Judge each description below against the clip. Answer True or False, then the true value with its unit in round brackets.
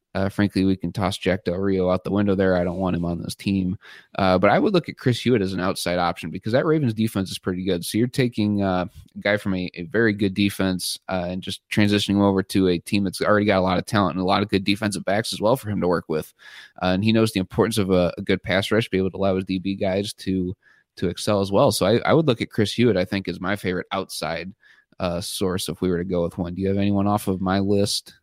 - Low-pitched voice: True (95 Hz)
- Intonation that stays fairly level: True (2.0 semitones)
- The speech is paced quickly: True (285 wpm)